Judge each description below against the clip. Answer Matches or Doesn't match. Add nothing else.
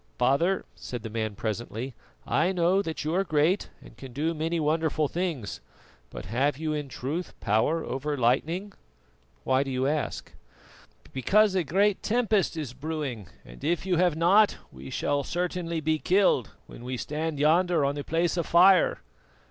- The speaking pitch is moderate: Matches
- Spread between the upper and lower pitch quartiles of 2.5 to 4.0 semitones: Doesn't match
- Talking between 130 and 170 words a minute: Matches